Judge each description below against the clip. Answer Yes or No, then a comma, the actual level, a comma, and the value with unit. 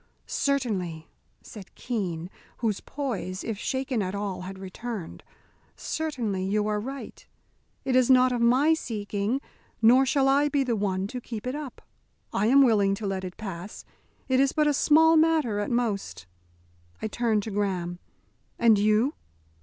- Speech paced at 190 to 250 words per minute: No, average, 160 wpm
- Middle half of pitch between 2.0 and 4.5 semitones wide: No, average, 5.0 semitones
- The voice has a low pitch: No, high, 225 Hz